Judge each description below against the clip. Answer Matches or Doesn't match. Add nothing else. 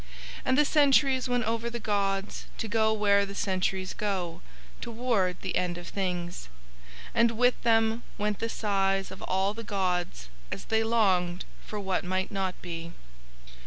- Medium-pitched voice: Doesn't match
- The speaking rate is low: Doesn't match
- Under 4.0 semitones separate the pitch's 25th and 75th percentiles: Matches